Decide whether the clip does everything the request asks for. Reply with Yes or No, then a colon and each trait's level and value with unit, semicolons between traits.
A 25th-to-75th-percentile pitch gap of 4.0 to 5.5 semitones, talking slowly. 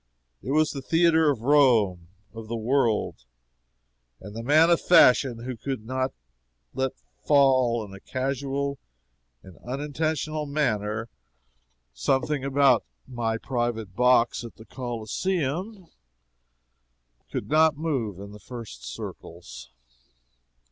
Yes: average, 4.3 semitones; slow, 115 wpm